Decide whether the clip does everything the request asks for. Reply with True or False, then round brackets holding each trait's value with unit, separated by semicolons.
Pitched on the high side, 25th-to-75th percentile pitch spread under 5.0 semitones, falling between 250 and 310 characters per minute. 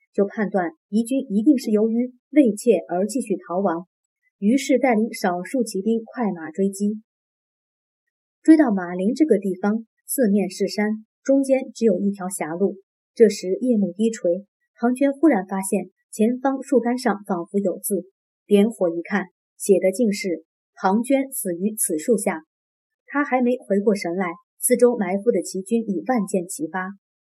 False (210 Hz; 4.6 semitones; 230 characters per minute)